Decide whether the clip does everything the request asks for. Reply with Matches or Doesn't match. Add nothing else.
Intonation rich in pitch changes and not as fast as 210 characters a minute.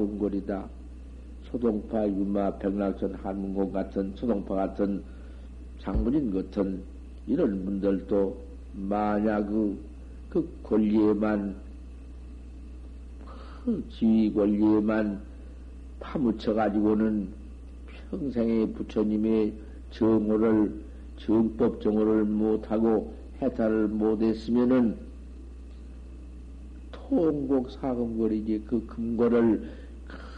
Matches